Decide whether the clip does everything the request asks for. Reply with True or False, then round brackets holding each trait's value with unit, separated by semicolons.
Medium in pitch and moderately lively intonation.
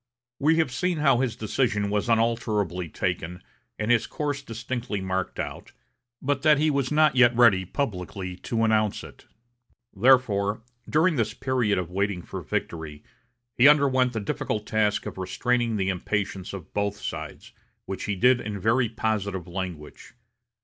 False (110 Hz; 4.9 semitones)